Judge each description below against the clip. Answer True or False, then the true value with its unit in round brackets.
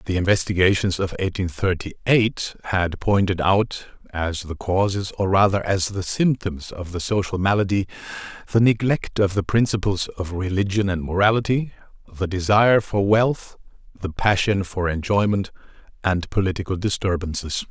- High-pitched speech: False (95 Hz)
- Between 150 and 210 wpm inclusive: False (140 wpm)